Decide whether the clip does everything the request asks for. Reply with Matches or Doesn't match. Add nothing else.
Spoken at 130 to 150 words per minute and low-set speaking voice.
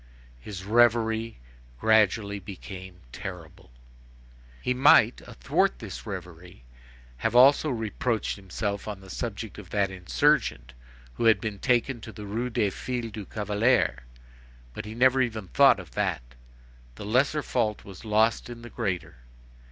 Matches